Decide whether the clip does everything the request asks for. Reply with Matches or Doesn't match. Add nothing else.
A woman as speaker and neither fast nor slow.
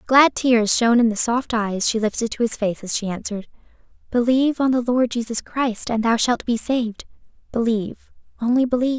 Matches